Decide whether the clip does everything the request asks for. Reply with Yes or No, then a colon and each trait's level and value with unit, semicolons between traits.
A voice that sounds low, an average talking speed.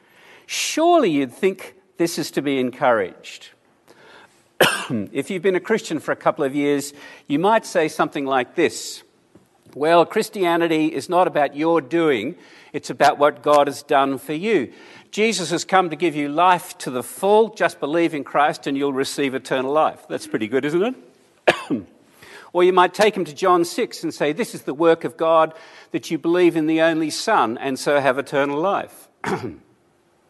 No: medium, 160 Hz; average, 180 wpm